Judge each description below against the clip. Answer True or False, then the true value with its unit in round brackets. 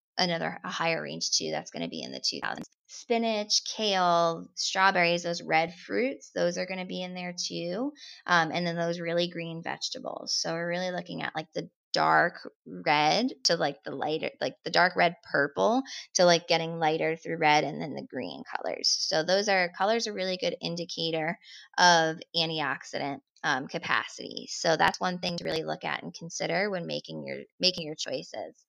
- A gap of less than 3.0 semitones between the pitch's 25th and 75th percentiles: True (2.4 semitones)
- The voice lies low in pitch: False (175 Hz)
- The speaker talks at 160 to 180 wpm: False (190 wpm)